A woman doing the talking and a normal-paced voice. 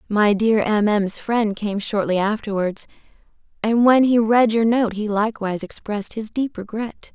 Yes: female; average, 170 wpm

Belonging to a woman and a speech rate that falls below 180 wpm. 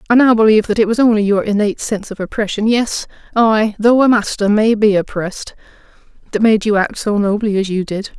No: female; average, 200 wpm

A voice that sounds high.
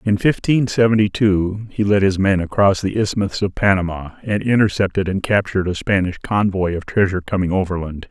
No: low, 100 Hz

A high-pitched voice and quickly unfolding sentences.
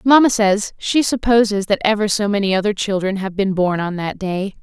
Yes: high, 205 Hz; fast, 210 wpm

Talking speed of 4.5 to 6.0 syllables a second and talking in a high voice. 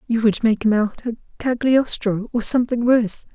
Yes: 5.3 syllables/s; high, 230 Hz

